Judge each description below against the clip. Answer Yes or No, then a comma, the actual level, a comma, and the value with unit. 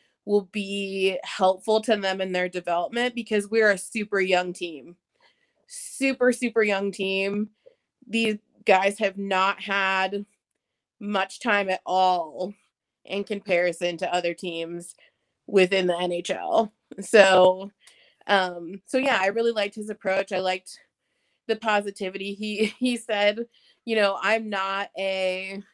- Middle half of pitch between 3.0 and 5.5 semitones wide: No, narrow, 2.4 semitones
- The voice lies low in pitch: No, high, 200 Hz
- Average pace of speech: No, slow, 130 wpm